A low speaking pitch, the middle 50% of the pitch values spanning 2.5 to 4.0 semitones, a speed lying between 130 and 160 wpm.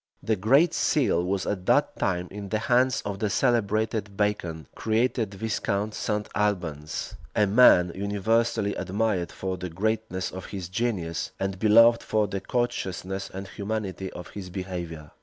Yes: low, 100 Hz; average, 2.9 semitones; average, 150 wpm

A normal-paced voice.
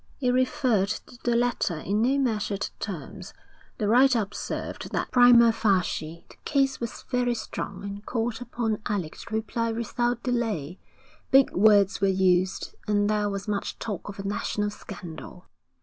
Yes: average, 155 wpm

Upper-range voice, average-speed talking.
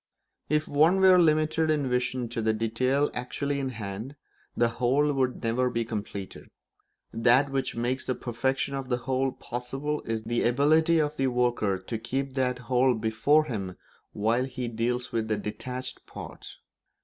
No: low, 125 Hz; average, 160 wpm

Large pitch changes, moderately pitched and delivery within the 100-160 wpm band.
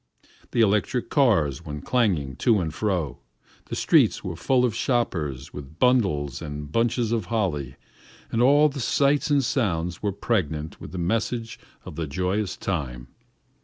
No: wide, 7.8 semitones; very low, 95 Hz; average, 155 wpm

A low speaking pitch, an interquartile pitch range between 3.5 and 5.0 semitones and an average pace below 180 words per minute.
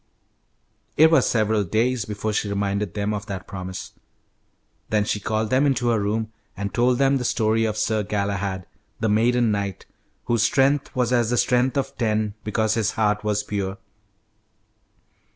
No: low, 110 Hz; average, 2.9 semitones; average, 165 wpm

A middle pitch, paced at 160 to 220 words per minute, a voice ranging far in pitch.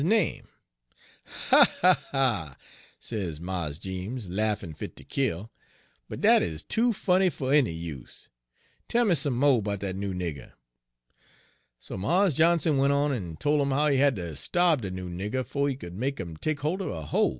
No: low, 115 Hz; average, 170 wpm; wide, 8.2 semitones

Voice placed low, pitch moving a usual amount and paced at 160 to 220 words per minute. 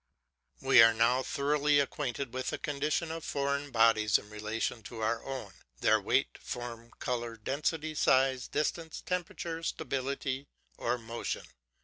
No: low, 130 Hz; average, 3.9 semitones; slow, 135 wpm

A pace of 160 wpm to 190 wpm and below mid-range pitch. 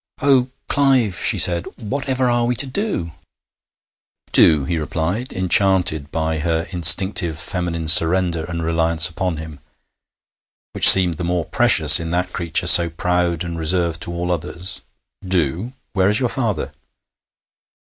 No: average, 140 wpm; very low, 85 Hz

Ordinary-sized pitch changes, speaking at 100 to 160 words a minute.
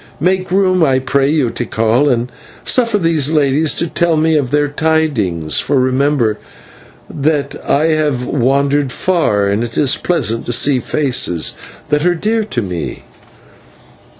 Yes: average, 4.4 semitones; average, 150 wpm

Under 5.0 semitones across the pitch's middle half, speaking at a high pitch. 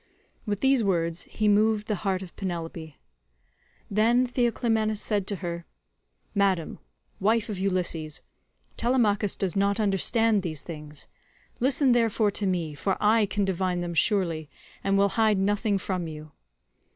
Yes: average, 3.6 semitones; high, 200 Hz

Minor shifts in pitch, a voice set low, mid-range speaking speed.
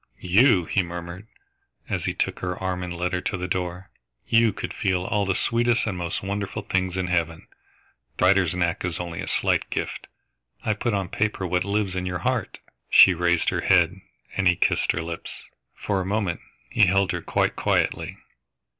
Yes: narrow, 2.1 semitones; very low, 90 Hz; average, 190 wpm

